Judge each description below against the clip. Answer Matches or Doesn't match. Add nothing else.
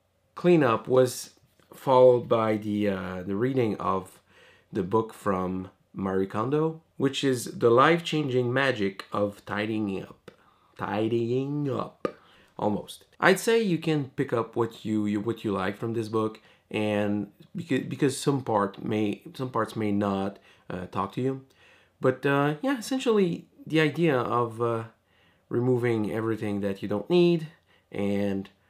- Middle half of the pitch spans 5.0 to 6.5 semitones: Matches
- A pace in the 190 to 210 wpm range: Doesn't match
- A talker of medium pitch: Doesn't match